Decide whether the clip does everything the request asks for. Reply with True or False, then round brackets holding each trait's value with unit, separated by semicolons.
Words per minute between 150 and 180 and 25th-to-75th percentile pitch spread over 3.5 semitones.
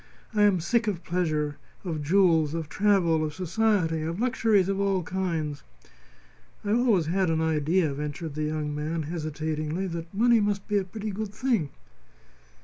True (160 wpm; 4.4 semitones)